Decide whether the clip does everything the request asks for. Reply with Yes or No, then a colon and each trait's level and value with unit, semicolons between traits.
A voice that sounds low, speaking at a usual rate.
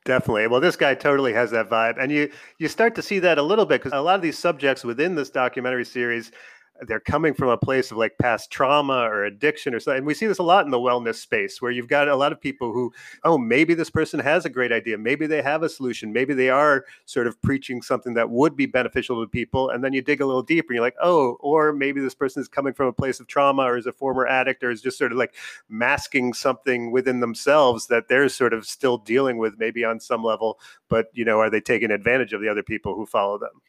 No: low, 130 Hz; fast, 260 wpm